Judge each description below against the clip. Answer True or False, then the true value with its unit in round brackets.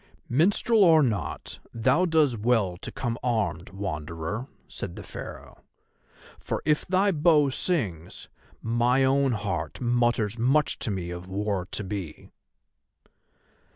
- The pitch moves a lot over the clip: True (6.3 semitones)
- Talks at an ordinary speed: False (125 wpm)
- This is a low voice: True (120 Hz)